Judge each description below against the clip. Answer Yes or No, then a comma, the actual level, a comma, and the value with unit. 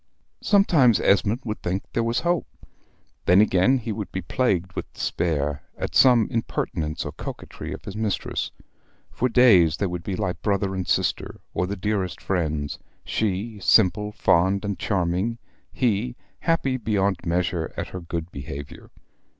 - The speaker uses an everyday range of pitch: Yes, average, 4.2 semitones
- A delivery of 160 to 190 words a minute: No, average, 150 wpm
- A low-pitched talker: Yes, low, 100 Hz